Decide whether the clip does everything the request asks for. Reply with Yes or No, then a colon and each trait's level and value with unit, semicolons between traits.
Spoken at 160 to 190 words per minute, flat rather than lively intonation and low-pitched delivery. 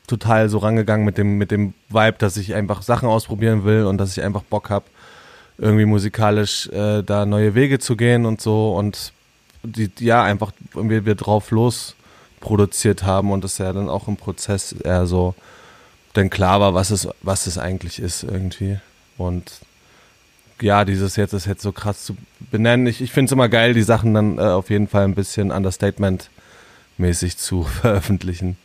Yes: average, 185 wpm; narrow, 2.1 semitones; low, 105 Hz